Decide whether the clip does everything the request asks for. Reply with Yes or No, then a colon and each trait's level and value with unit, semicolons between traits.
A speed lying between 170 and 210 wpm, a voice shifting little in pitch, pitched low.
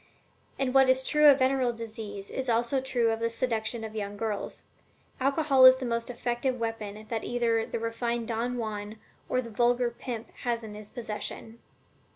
No: average, 180 wpm; narrow, 2.3 semitones; high, 235 Hz